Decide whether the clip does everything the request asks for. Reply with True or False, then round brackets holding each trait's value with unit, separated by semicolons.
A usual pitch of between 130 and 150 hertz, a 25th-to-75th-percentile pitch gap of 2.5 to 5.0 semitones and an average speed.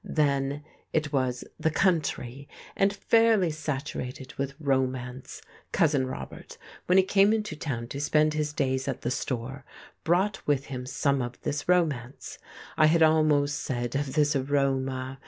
True (140 Hz; 3.0 semitones; 150 wpm)